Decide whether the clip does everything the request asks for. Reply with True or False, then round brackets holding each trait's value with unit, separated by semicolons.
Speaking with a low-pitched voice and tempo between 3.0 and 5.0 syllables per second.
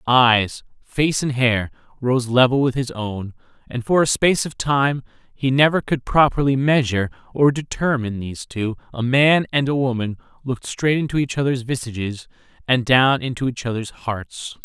True (125 Hz; 4.9 syllables/s)